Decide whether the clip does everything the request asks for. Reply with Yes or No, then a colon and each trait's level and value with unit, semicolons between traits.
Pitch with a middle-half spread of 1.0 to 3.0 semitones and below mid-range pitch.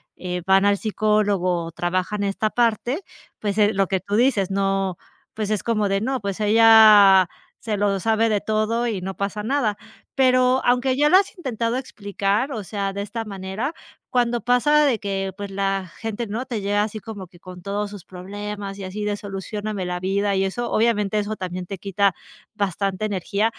No: narrow, 2.5 semitones; high, 205 Hz